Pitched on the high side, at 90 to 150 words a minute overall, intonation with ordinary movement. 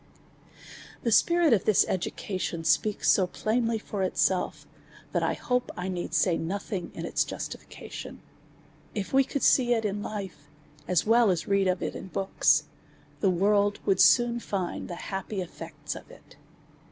No: high, 200 Hz; average, 165 wpm; average, 3.4 semitones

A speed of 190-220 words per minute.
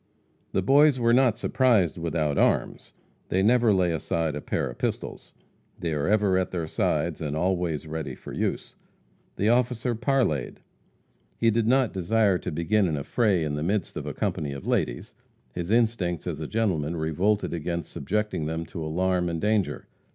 No: average, 175 wpm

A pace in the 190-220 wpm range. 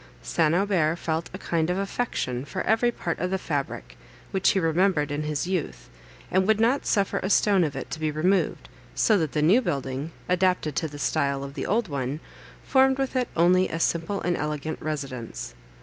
Yes: average, 195 wpm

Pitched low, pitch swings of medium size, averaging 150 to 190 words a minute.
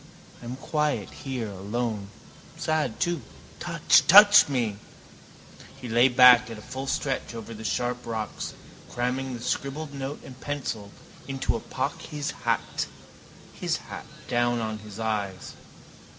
No: low, 125 Hz; average, 3.5 semitones; slow, 135 wpm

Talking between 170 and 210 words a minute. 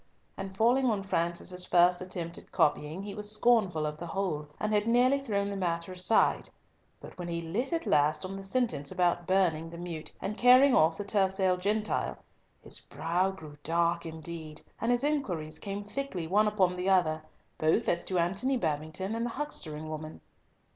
Yes: average, 180 wpm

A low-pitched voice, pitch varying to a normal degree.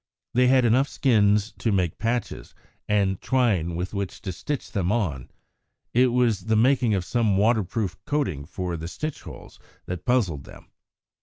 Yes: low, 105 Hz; average, 5.0 semitones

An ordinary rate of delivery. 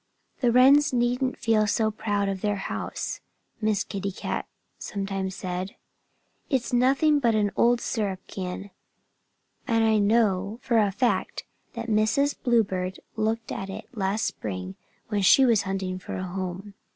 Yes: average, 150 wpm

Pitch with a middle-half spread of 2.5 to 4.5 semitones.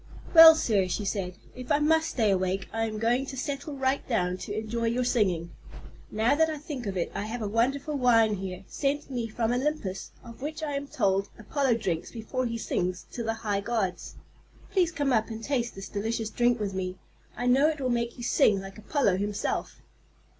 No: average, 5.0 semitones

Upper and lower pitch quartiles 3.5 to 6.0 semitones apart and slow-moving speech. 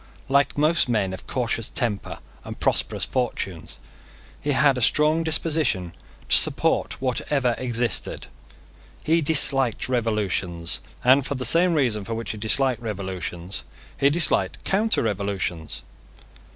Yes: wide, 5.6 semitones; slow, 125 wpm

